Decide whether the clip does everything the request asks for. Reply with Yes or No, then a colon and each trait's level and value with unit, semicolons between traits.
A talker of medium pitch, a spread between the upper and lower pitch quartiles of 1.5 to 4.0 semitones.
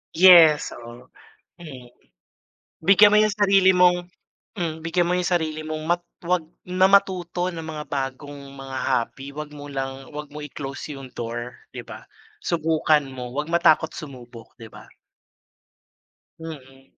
No: medium, 155 Hz; average, 4.5 semitones